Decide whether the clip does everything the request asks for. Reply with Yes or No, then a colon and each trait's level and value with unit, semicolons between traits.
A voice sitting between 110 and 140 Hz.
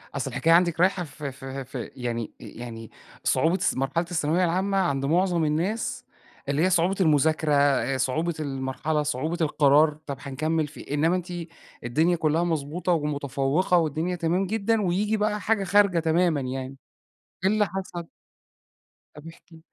No: medium, 160 Hz